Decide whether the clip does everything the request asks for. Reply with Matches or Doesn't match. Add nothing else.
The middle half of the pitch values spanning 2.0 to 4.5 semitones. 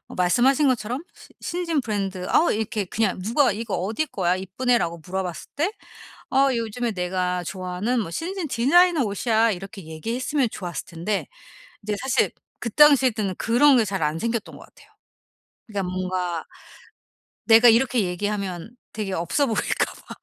Doesn't match